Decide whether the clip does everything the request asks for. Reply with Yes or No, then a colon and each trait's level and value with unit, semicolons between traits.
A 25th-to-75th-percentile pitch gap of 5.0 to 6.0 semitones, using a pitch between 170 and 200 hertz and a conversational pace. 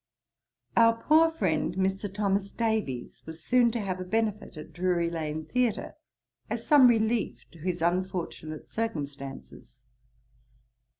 No: wide, 5.5 semitones; high, 190 Hz; slow, 125 wpm